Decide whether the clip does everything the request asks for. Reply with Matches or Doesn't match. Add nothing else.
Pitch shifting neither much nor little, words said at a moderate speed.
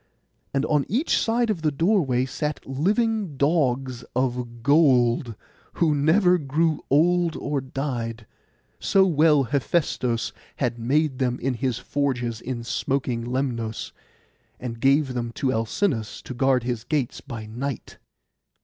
Doesn't match